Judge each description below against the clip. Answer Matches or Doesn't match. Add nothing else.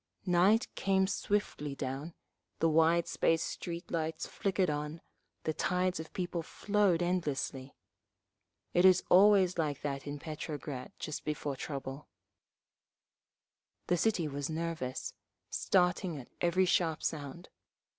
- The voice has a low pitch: Doesn't match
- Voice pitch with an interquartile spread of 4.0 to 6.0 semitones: Doesn't match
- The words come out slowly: Matches